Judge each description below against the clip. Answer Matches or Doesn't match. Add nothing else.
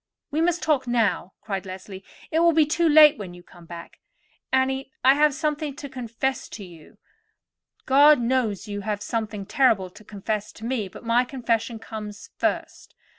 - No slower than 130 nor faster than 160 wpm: Doesn't match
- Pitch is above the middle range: Matches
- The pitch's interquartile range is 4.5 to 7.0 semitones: Matches